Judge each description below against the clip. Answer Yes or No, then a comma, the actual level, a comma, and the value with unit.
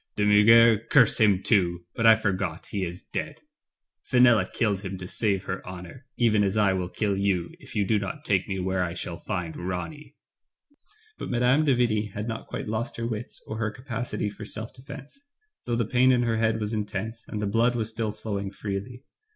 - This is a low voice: Yes, low, 105 Hz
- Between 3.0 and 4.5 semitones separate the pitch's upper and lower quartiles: Yes, average, 3.3 semitones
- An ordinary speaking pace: No, fast, 215 wpm